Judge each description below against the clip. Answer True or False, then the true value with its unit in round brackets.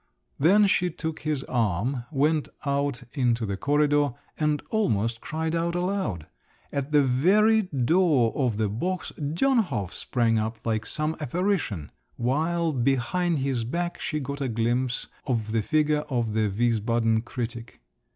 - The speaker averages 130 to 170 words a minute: True (140 wpm)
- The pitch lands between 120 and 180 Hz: True (135 Hz)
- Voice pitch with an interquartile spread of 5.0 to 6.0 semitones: True (5.6 semitones)